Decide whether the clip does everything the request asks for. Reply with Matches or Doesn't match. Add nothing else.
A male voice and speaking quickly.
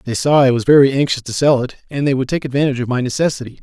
Matches